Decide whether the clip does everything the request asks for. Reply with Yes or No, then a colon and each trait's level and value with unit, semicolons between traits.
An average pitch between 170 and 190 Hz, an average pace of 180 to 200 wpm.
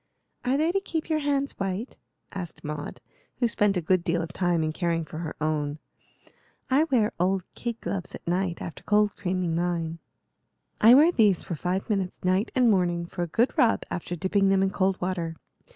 Yes: medium, 185 Hz; average, 195 wpm